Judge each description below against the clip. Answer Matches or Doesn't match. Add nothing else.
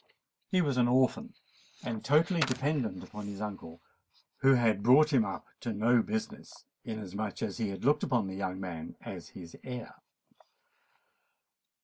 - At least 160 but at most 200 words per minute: Doesn't match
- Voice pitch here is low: Matches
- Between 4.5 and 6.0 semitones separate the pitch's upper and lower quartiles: Matches